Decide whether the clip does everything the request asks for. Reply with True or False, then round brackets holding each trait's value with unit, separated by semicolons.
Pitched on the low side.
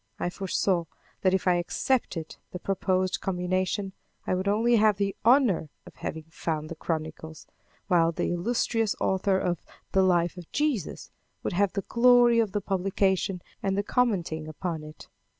False (185 Hz)